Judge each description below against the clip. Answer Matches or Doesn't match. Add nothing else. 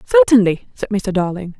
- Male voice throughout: Doesn't match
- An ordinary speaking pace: Matches